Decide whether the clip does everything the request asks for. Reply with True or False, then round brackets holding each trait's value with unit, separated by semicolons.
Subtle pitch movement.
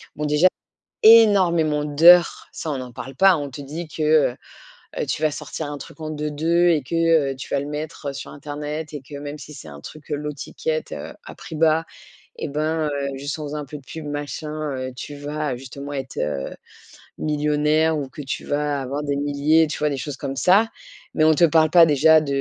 True (1.9 semitones)